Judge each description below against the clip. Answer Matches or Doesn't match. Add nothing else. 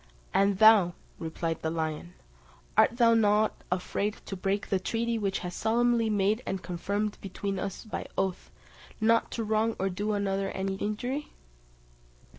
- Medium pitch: Doesn't match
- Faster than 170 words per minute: Doesn't match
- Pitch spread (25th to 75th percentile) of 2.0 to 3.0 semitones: Matches